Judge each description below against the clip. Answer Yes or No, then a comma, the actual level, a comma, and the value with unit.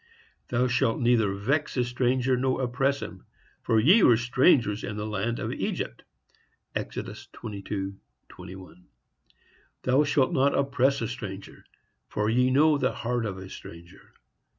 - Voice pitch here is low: Yes, low, 120 Hz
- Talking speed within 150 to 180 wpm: No, slow, 135 wpm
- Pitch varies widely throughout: No, average, 4.4 semitones